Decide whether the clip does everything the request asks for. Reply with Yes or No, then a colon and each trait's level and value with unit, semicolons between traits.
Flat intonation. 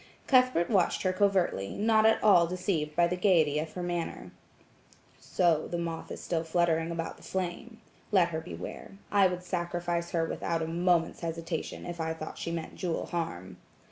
Yes: narrow, 1.9 semitones